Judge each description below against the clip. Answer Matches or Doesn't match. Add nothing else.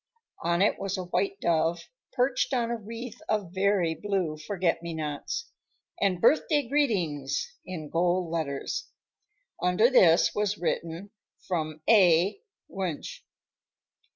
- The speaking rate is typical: Doesn't match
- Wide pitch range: Doesn't match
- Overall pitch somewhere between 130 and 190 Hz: Matches